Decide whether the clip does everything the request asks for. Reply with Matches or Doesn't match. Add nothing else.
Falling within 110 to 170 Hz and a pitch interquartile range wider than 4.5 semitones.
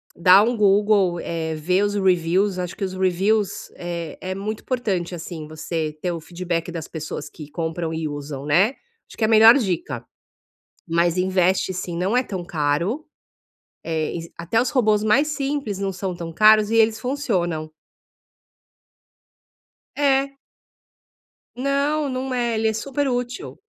Doesn't match